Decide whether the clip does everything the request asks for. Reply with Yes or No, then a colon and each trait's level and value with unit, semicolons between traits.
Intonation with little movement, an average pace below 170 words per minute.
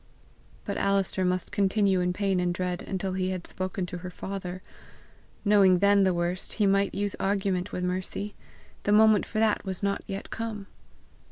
No: narrow, 1.8 semitones; average, 175 wpm